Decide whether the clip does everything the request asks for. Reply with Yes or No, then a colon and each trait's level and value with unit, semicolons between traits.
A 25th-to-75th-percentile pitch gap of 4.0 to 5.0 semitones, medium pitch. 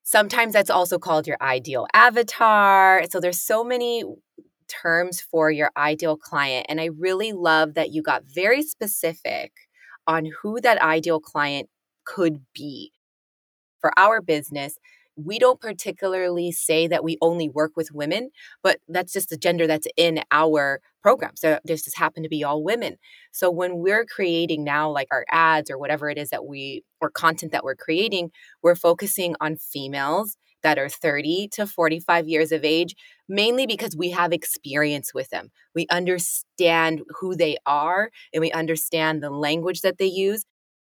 No: average, 3.4 semitones; medium, 165 Hz